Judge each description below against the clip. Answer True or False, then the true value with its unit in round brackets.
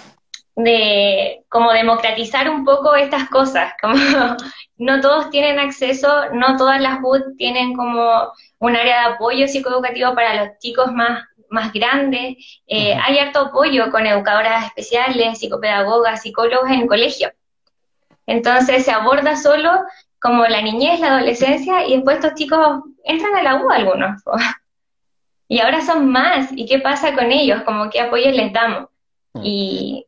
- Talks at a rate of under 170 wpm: True (150 wpm)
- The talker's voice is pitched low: False (260 Hz)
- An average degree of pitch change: True (3.4 semitones)